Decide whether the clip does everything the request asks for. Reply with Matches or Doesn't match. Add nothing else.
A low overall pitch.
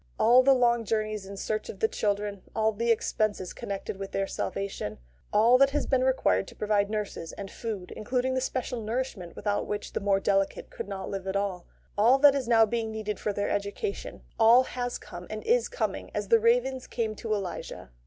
Doesn't match